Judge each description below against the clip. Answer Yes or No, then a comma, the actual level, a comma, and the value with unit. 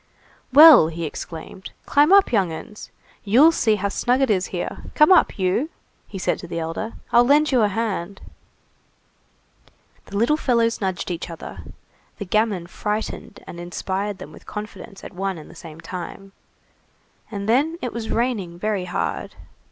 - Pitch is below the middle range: No, high, 205 Hz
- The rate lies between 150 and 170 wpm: Yes, average, 165 wpm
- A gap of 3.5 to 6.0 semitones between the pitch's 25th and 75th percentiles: Yes, average, 4.7 semitones